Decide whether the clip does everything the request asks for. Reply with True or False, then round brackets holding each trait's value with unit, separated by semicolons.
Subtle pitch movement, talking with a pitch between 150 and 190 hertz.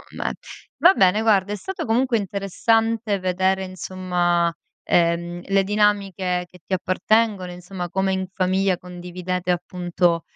True (2.2 semitones; 185 Hz)